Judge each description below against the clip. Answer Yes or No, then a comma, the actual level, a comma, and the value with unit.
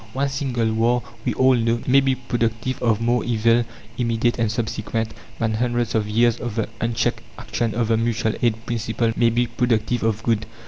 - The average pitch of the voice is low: Yes, low, 115 Hz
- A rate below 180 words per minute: No, average, 185 wpm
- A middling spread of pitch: No, narrow, 1.2 semitones